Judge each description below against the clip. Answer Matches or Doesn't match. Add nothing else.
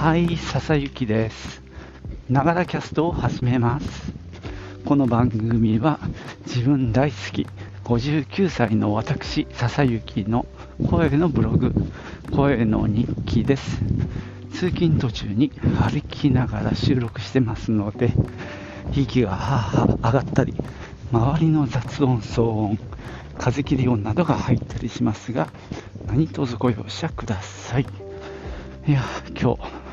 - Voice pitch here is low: Matches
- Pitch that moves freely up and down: Doesn't match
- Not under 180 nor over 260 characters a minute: Matches